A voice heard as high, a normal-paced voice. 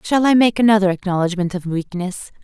Yes: high, 195 Hz; average, 175 wpm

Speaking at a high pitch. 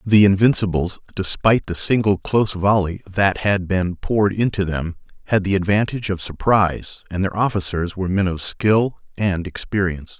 No: very low, 95 Hz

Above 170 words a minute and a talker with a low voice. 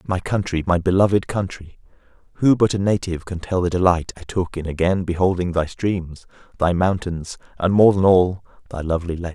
Yes: average, 185 wpm; very low, 90 Hz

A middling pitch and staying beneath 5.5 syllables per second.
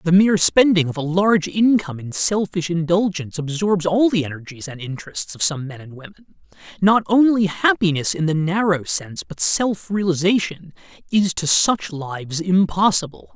Yes: medium, 175 Hz; 5.2 syllables/s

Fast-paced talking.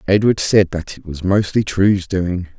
No: average, 185 wpm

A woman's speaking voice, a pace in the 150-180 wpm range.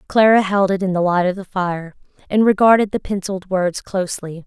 No: female; average, 200 wpm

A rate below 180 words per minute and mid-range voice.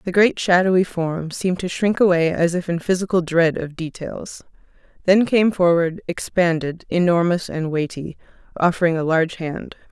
Yes: average, 155 wpm; medium, 175 Hz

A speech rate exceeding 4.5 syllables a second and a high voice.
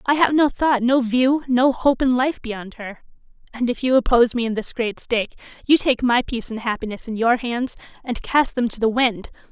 Yes: 5.2 syllables/s; high, 245 Hz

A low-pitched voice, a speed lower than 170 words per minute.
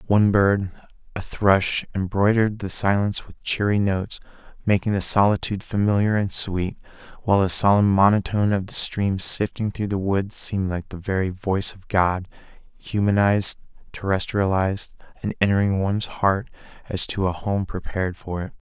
Yes: low, 100 Hz; average, 150 wpm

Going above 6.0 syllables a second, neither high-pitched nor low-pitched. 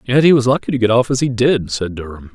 No: 6.4 syllables/s; low, 120 Hz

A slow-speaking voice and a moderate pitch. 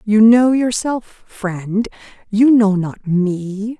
No: slow, 125 wpm; high, 215 Hz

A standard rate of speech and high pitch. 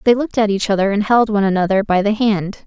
No: fast, 270 wpm; high, 210 Hz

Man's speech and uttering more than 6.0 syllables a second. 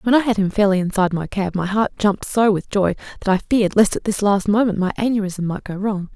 No: female; 6.2 syllables/s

